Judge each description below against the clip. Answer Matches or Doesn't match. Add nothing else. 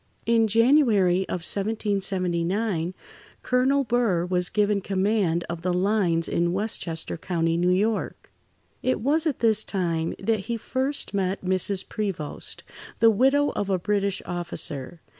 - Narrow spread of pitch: Doesn't match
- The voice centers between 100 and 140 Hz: Doesn't match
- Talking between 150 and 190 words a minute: Doesn't match